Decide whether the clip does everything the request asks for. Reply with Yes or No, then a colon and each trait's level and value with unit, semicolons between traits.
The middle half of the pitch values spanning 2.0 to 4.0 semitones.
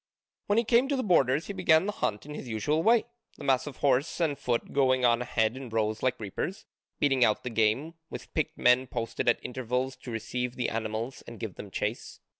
No: average, 4.7 semitones